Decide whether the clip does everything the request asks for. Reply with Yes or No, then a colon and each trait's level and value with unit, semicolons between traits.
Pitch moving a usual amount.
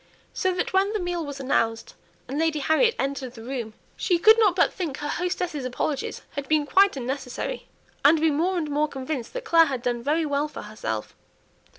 Yes: average, 5.0 semitones